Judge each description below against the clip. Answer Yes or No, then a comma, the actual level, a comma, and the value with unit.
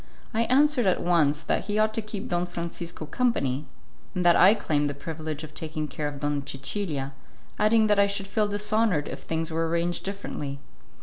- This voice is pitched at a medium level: Yes, medium, 175 Hz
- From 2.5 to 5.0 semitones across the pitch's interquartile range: No, wide, 5.5 semitones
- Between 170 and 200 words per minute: Yes, average, 190 wpm